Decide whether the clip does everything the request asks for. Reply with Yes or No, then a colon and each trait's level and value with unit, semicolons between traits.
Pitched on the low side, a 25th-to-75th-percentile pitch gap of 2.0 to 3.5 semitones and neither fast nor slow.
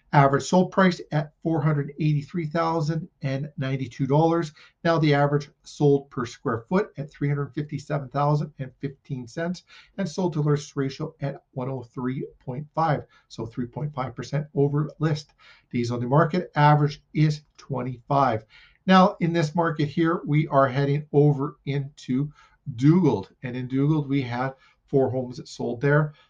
No: medium, 145 Hz; narrow, 2.5 semitones; average, 160 wpm